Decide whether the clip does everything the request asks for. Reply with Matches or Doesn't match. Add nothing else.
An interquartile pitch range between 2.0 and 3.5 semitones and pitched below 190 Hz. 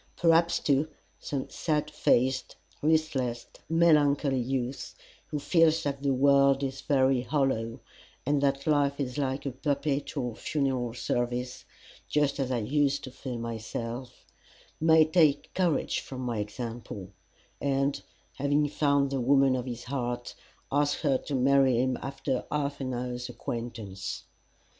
Matches